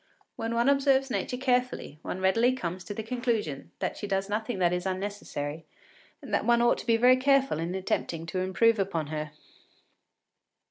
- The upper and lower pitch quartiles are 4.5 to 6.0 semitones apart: Yes, wide, 5.6 semitones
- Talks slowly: No, average, 180 wpm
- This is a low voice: No, high, 205 Hz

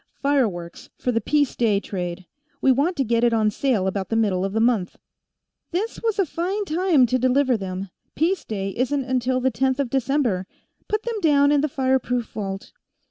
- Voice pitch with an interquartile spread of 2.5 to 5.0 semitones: No, wide, 5.4 semitones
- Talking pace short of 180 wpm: No, average, 190 wpm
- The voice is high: Yes, very high, 255 Hz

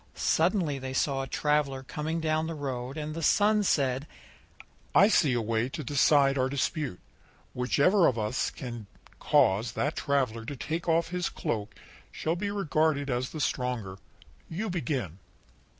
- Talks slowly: No, average, 155 wpm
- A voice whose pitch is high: No, medium, 140 Hz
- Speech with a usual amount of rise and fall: Yes, average, 4.3 semitones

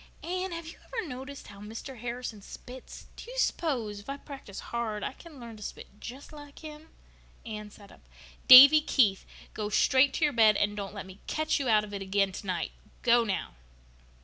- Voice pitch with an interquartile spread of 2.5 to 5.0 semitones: No, wide, 5.5 semitones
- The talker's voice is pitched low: No, high, 240 Hz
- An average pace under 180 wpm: No, fast, 205 wpm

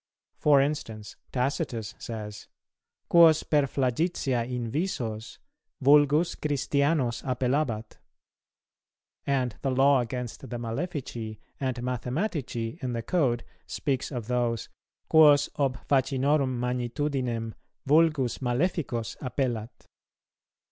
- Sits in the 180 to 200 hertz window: No, low, 130 Hz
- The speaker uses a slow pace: Yes, slow, 95 wpm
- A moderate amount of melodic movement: Yes, average, 3.5 semitones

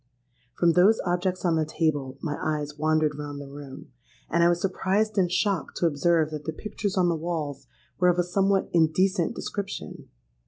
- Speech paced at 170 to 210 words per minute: Yes, average, 185 wpm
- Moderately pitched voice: Yes, medium, 170 Hz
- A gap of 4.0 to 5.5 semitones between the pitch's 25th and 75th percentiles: No, average, 3.4 semitones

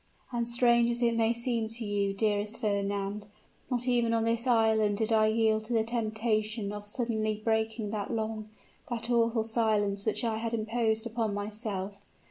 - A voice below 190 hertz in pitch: No, high, 220 Hz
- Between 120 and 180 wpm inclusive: Yes, average, 170 wpm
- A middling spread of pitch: No, narrow, 1.7 semitones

